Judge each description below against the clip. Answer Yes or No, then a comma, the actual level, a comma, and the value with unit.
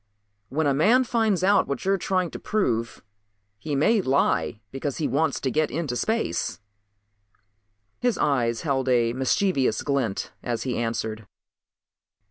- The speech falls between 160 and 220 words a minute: No, average, 145 wpm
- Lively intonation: Yes, wide, 7.3 semitones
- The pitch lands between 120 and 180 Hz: Yes, medium, 140 Hz